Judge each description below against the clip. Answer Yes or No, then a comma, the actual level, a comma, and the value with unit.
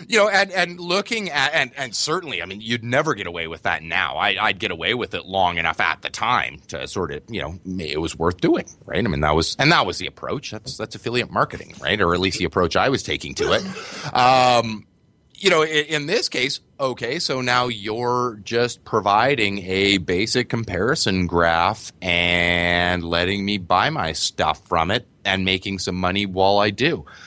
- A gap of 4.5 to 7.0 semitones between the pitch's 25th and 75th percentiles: Yes, wide, 5.5 semitones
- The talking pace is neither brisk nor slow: No, fast, 210 wpm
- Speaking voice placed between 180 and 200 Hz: No, low, 100 Hz